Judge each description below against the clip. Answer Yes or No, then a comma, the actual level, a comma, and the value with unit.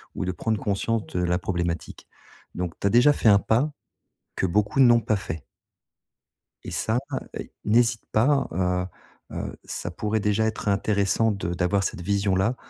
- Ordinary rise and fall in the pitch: Yes, average, 3.6 semitones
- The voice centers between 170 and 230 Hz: No, low, 100 Hz